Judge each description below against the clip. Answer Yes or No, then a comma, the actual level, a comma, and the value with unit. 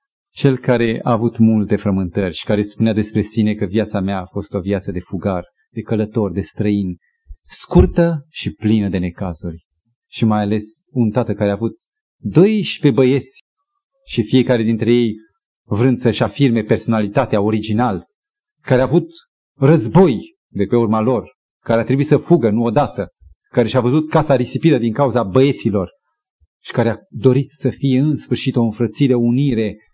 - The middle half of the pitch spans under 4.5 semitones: No, average, 4.8 semitones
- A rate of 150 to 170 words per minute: Yes, average, 165 wpm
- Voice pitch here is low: Yes, low, 115 Hz